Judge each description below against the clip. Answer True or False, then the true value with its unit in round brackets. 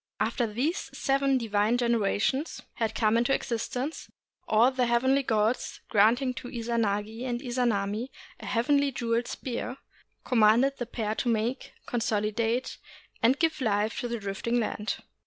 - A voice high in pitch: True (235 Hz)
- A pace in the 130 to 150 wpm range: True (140 wpm)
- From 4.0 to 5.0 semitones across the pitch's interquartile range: False (2.7 semitones)